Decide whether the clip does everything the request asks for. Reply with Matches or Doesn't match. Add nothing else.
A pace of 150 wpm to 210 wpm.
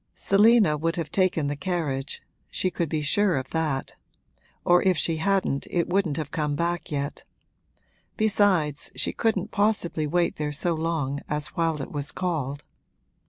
Matches